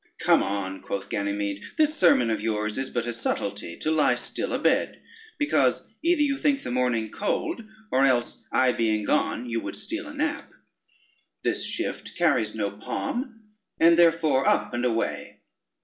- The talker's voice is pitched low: Yes, low, 125 Hz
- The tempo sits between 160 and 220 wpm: Yes, average, 165 wpm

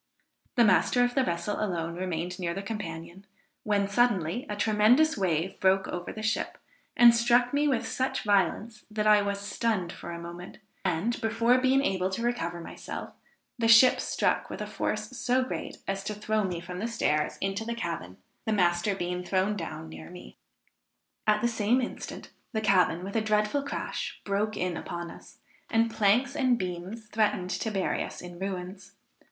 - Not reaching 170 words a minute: No, average, 180 wpm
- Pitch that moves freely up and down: No, average, 4.3 semitones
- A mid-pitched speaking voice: No, high, 205 Hz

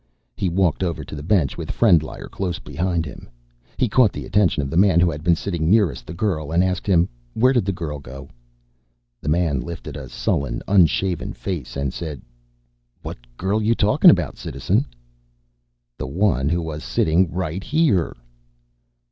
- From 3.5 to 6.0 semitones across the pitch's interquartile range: Yes, average, 4.1 semitones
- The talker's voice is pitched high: No, very low, 85 Hz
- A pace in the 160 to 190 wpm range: Yes, average, 175 wpm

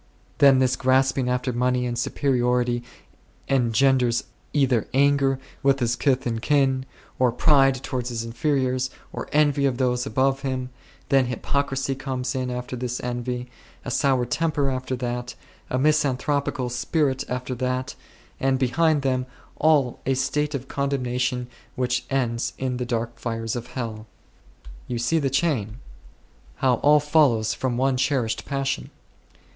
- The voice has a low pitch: Yes, low, 130 Hz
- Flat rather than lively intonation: Yes, narrow, 1.9 semitones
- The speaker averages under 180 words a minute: Yes, average, 145 wpm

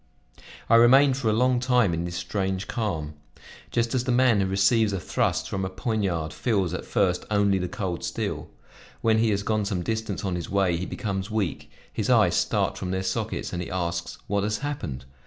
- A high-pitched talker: No, low, 100 Hz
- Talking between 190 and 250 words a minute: Yes, fast, 205 wpm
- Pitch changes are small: No, average, 3.7 semitones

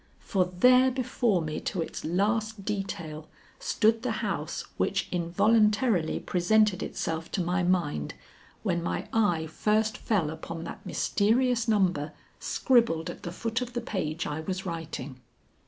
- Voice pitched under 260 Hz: Yes, high, 190 Hz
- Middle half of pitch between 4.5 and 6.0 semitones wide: Yes, average, 5.0 semitones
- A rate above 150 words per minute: No, average, 140 wpm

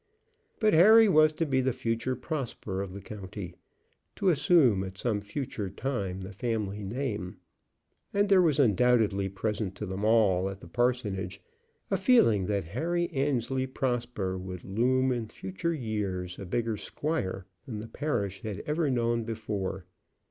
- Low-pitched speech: Yes, low, 115 Hz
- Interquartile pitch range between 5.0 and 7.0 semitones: Yes, wide, 5.5 semitones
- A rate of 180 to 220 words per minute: No, average, 155 wpm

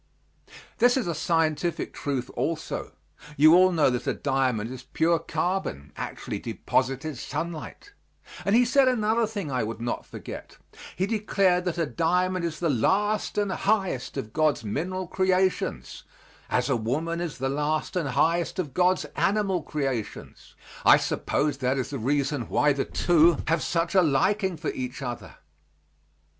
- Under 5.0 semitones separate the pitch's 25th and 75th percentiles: No, wide, 5.6 semitones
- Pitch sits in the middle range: Yes, medium, 160 Hz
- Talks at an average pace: Yes, average, 155 wpm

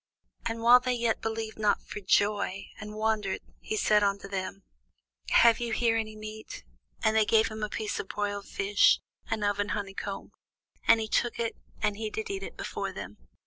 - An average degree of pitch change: No, narrow, 1.6 semitones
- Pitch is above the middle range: Yes, high, 215 Hz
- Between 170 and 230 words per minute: Yes, average, 185 wpm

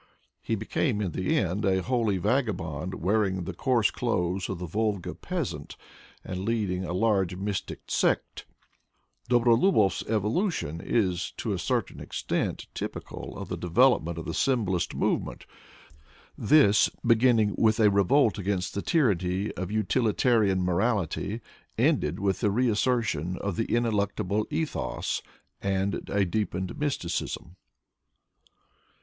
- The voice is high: No, low, 100 Hz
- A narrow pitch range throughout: No, average, 3.9 semitones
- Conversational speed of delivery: No, slow, 130 wpm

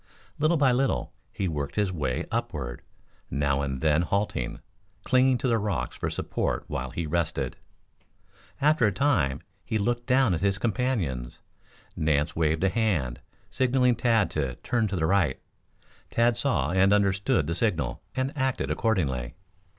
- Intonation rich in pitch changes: Yes, wide, 7.9 semitones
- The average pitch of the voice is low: Yes, low, 100 Hz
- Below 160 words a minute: Yes, average, 150 wpm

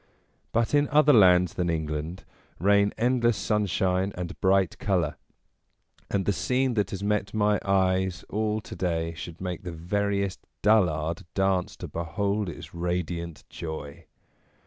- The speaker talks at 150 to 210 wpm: No, average, 140 wpm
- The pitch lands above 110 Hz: No, very low, 95 Hz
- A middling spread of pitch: Yes, average, 3.2 semitones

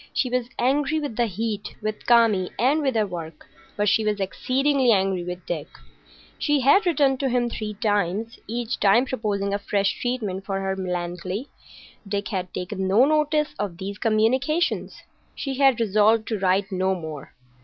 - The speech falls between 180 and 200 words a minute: No, average, 165 wpm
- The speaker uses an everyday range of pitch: Yes, average, 4.9 semitones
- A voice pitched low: No, high, 215 Hz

